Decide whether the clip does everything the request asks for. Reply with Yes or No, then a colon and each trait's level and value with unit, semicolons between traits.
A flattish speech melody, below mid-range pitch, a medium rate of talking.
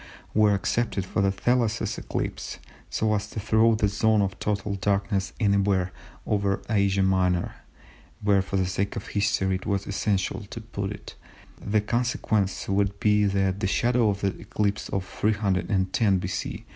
Yes: narrow, 1.6 semitones; low, 100 Hz; average, 160 wpm